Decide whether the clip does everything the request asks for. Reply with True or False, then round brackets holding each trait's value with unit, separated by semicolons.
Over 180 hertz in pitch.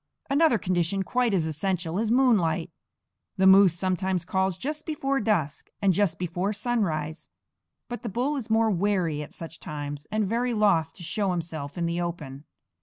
True (190 Hz)